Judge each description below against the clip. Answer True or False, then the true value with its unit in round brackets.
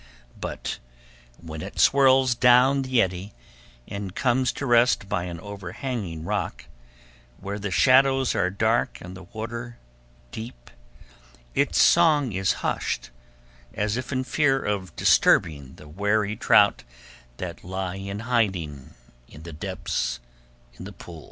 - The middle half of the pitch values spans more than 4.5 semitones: True (5.6 semitones)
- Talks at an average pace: False (130 wpm)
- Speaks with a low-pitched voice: True (105 Hz)